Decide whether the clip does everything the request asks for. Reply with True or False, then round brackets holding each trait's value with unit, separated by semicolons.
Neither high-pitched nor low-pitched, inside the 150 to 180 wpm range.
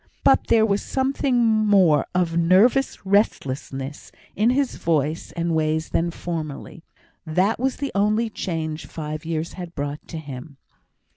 False (170 Hz; 140 wpm)